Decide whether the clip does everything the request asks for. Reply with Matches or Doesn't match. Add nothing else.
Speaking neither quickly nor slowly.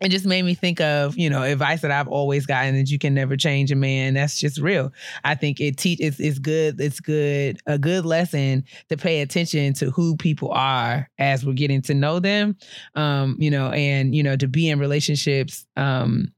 Doesn't match